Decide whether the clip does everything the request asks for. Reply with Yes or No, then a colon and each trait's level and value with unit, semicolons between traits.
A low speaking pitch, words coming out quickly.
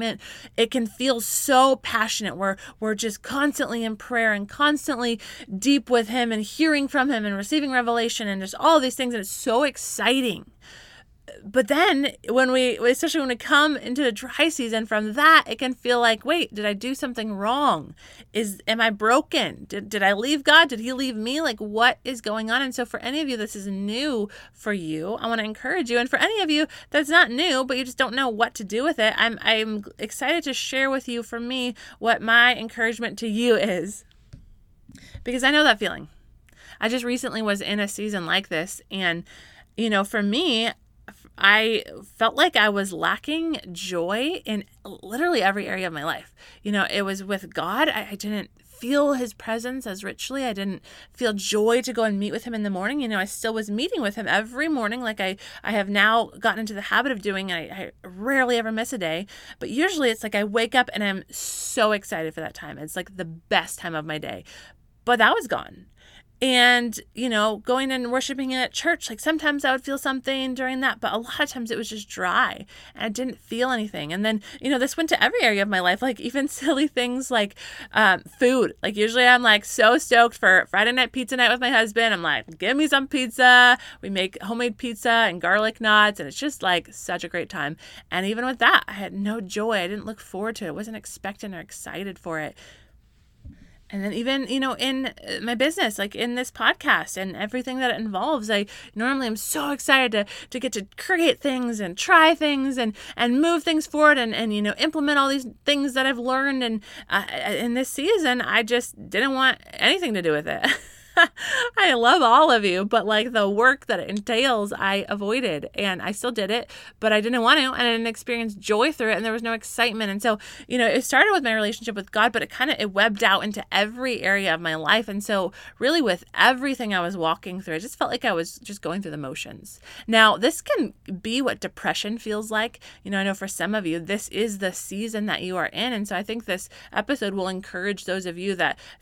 No: high, 230 Hz; fast, 225 wpm